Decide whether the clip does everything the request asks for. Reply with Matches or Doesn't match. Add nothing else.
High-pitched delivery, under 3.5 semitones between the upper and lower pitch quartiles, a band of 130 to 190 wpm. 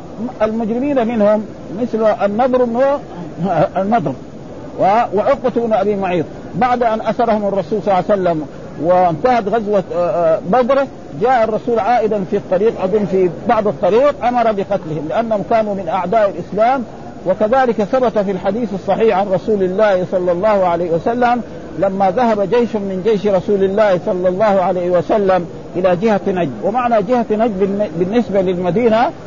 Doesn't match